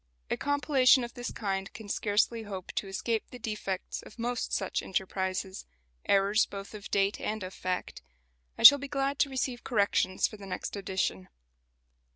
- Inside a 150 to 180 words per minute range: Yes, average, 170 wpm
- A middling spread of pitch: Yes, average, 4.0 semitones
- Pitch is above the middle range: Yes, high, 210 Hz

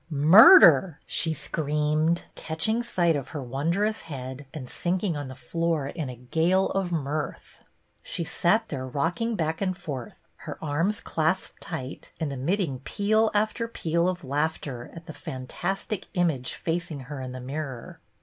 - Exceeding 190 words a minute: No, average, 150 wpm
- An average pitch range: Yes, average, 4.5 semitones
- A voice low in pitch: No, medium, 160 Hz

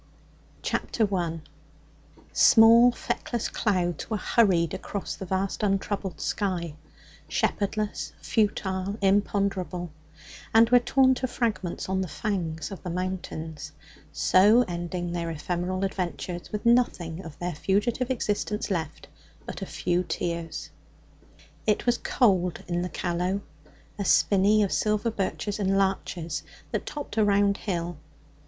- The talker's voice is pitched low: No, high, 190 Hz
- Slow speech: Yes, slow, 130 wpm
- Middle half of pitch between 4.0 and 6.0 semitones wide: No, average, 3.2 semitones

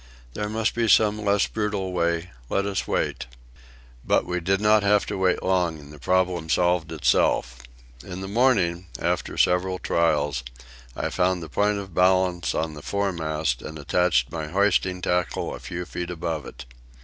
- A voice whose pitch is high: No, very low, 90 Hz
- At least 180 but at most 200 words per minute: No, average, 170 wpm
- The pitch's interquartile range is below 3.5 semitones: Yes, average, 3.1 semitones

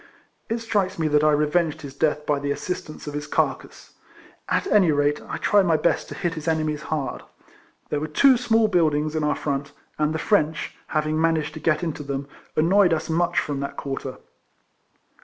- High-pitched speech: No, medium, 155 Hz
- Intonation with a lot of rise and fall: No, narrow, 2.6 semitones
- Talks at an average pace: Yes, average, 195 wpm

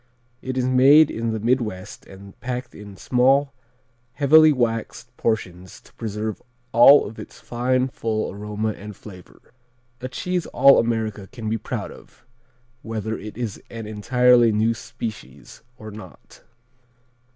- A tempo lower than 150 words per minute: Yes, average, 140 wpm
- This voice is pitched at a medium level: No, low, 115 Hz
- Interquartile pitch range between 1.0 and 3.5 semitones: Yes, average, 3.1 semitones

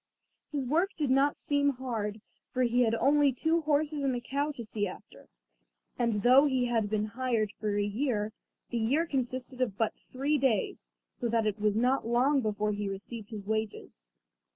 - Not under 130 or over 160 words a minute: No, average, 185 wpm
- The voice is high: Yes, high, 240 Hz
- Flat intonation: No, average, 4.4 semitones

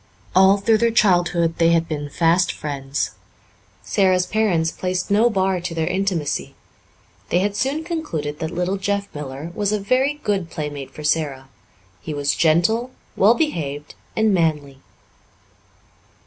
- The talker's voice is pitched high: No, medium, 175 Hz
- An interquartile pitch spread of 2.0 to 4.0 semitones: No, average, 4.9 semitones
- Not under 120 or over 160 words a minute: Yes, average, 145 wpm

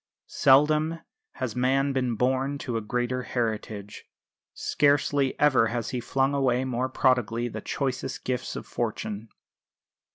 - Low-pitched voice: Yes, low, 130 Hz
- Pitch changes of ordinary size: No, narrow, 2.3 semitones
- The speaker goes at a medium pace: No, slow, 130 wpm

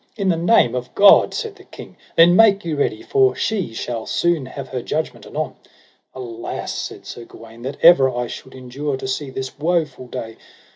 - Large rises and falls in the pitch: Yes, wide, 5.9 semitones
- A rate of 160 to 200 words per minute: Yes, average, 190 wpm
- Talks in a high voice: No, medium, 140 Hz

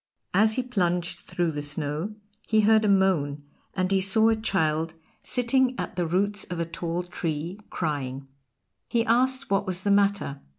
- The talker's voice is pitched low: No, medium, 185 Hz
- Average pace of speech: Yes, average, 170 wpm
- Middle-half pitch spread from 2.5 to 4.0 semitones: No, average, 4.8 semitones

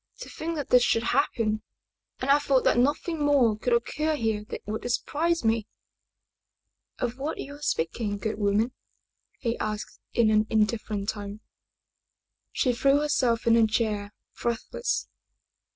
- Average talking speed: Yes, average, 150 wpm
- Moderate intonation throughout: Yes, average, 4.5 semitones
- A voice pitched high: Yes, high, 235 Hz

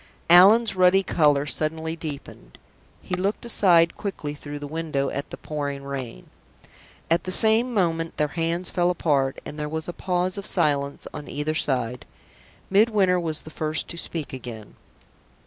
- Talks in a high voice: No, medium, 160 Hz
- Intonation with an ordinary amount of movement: Yes, average, 3.8 semitones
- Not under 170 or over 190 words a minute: No, average, 160 wpm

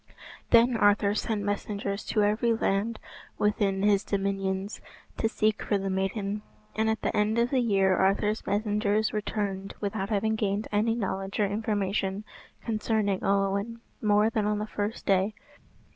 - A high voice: Yes, high, 205 Hz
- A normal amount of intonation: No, narrow, 1.7 semitones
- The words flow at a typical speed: Yes, average, 150 wpm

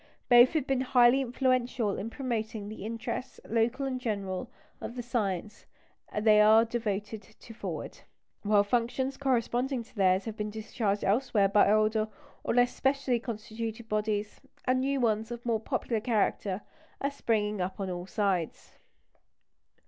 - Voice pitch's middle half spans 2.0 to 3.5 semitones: Yes, average, 2.8 semitones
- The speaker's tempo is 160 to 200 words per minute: No, average, 150 wpm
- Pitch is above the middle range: Yes, high, 225 Hz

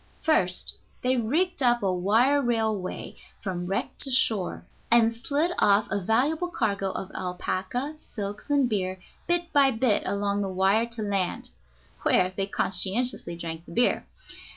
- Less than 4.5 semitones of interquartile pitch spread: No, average, 4.9 semitones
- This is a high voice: Yes, high, 215 Hz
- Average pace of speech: Yes, average, 150 wpm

